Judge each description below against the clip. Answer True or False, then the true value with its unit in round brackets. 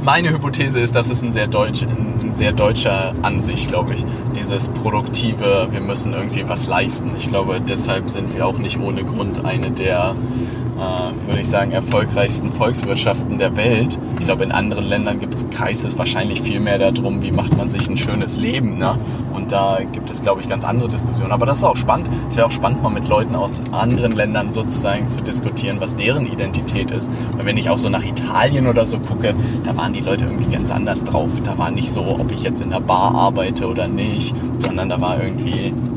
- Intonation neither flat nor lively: False (1.3 semitones)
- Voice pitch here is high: False (120 Hz)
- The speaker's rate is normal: False (205 wpm)